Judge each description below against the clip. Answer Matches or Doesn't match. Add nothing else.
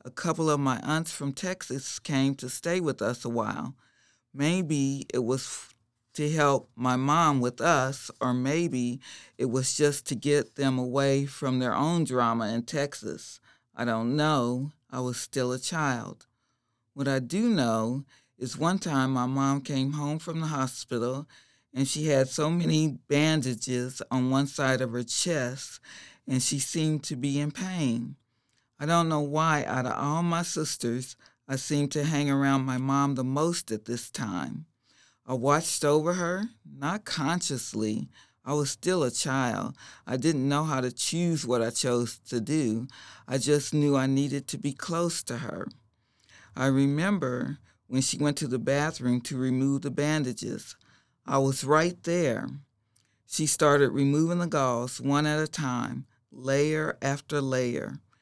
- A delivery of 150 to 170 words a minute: Matches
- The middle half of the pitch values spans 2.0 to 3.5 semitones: Matches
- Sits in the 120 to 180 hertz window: Matches